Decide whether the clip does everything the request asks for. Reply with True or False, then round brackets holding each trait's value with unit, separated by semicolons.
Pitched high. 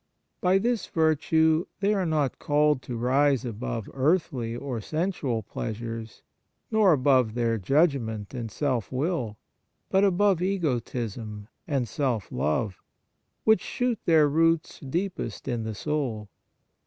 False (140 Hz)